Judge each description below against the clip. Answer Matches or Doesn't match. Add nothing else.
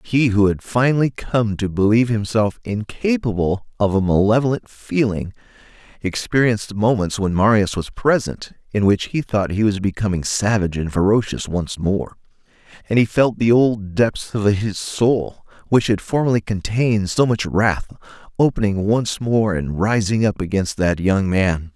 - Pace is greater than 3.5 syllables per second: Matches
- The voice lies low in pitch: Matches